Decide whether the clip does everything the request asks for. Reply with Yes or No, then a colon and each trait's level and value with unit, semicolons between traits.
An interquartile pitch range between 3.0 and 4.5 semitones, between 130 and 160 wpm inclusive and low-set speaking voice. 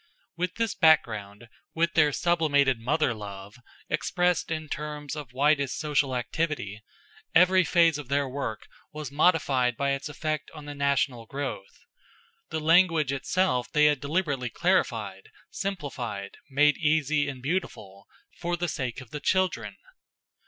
No: average, 4.2 semitones; average, 140 wpm; medium, 145 Hz